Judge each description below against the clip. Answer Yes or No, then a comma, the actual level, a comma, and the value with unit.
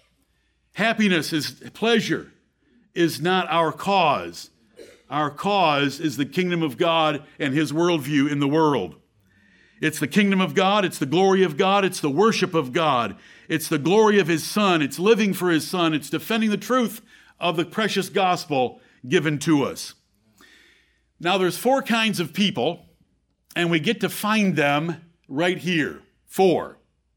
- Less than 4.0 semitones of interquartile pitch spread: No, average, 4.4 semitones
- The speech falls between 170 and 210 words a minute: No, average, 160 wpm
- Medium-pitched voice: Yes, medium, 175 Hz